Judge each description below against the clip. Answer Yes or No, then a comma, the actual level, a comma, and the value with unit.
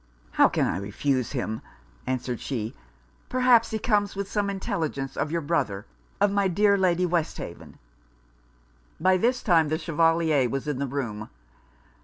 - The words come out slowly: No, average, 150 wpm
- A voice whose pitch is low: No, medium, 165 Hz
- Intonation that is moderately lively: No, wide, 6.7 semitones